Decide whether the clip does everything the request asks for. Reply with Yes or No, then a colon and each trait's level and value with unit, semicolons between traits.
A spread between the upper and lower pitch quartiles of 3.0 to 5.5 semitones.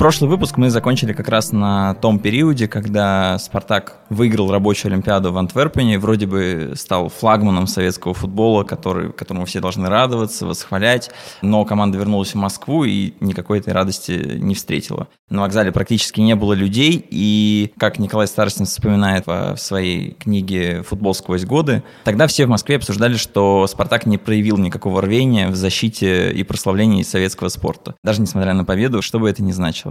No: narrow, 2.6 semitones